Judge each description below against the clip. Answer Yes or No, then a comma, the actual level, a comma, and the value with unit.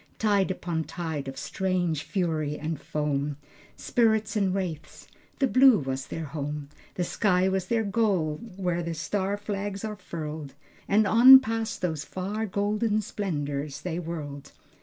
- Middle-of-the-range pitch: Yes, medium, 180 Hz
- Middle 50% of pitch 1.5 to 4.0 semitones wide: No, average, 5.1 semitones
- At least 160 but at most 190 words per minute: No, average, 145 wpm